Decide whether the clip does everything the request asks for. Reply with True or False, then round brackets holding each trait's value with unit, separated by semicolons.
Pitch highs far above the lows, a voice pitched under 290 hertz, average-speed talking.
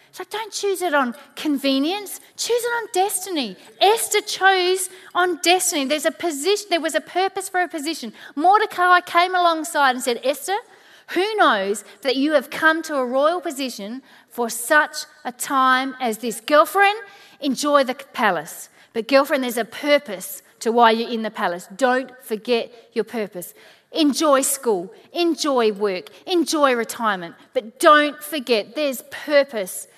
False (6.6 semitones; 295 Hz; 150 wpm)